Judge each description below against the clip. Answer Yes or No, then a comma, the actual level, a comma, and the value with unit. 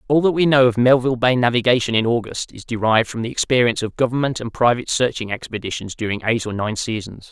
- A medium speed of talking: No, fast, 215 wpm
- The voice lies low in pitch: Yes, low, 120 Hz